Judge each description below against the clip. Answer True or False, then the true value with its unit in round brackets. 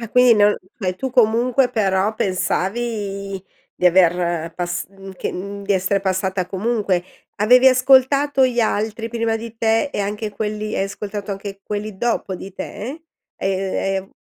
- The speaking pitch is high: True (205 Hz)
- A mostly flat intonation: False (3.3 semitones)